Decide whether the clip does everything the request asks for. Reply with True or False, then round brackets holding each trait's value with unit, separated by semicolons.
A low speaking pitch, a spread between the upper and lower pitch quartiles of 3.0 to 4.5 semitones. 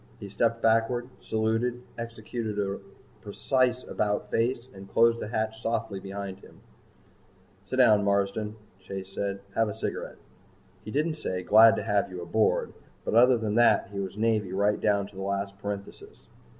False (105 Hz; 2.6 semitones)